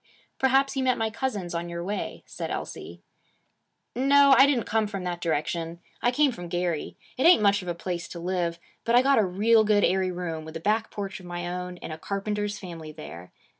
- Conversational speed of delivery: No, fast, 215 wpm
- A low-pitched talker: No, high, 190 Hz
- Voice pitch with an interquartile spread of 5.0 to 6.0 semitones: No, average, 4.6 semitones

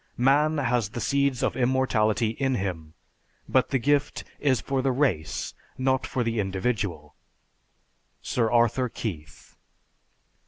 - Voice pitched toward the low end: Yes, low, 120 Hz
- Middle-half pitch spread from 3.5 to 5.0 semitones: Yes, average, 3.9 semitones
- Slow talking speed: Yes, slow, 125 wpm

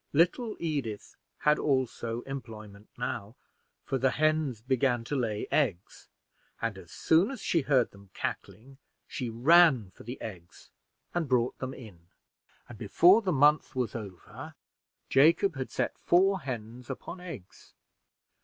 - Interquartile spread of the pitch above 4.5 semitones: Yes, wide, 5.6 semitones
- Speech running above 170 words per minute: No, average, 140 wpm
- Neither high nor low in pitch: No, low, 130 Hz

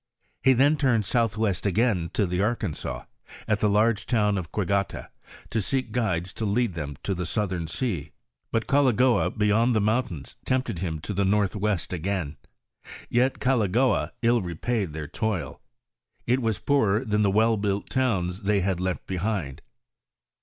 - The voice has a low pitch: Yes, low, 105 Hz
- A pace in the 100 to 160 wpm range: Yes, average, 155 wpm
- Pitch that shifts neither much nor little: Yes, average, 4.1 semitones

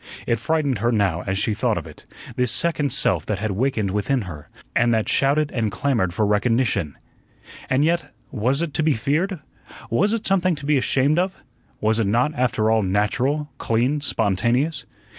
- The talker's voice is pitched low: Yes, low, 125 Hz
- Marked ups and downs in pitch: Yes, wide, 5.7 semitones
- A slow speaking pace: No, average, 180 wpm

